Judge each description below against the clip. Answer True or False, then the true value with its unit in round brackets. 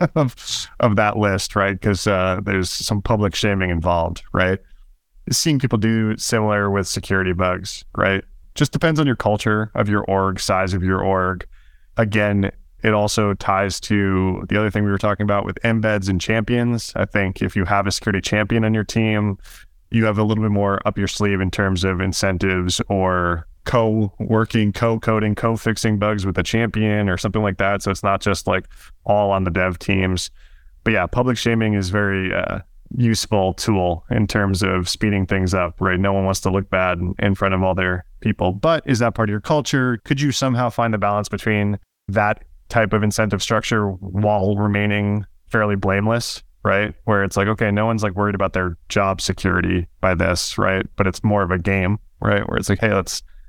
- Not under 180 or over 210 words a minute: True (200 wpm)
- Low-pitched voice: True (100 Hz)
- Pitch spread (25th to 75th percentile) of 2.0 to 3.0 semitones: True (2.5 semitones)